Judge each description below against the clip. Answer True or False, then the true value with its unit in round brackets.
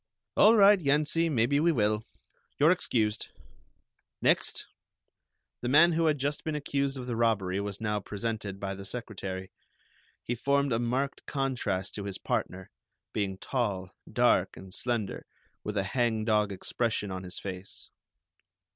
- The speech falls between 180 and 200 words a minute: False (145 wpm)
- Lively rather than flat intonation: True (5.9 semitones)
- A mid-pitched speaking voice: False (115 Hz)